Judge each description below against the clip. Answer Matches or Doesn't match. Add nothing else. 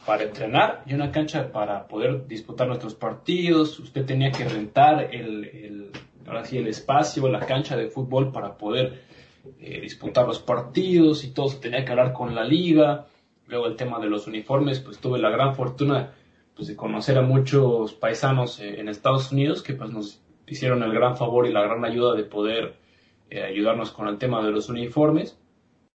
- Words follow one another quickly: Doesn't match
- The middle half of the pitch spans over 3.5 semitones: Matches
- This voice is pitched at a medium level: Doesn't match